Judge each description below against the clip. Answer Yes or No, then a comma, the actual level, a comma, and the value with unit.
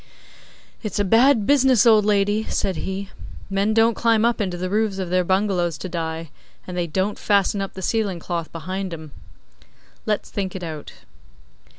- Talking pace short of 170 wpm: No, average, 175 wpm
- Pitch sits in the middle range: No, high, 195 Hz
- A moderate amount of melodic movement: Yes, average, 3.2 semitones